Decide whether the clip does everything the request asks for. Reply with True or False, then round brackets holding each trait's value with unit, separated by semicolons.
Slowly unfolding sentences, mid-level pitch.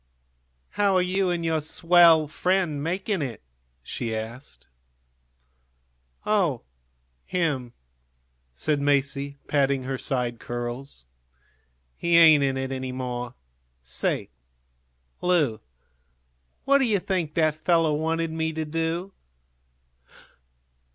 True (105 wpm; 155 Hz)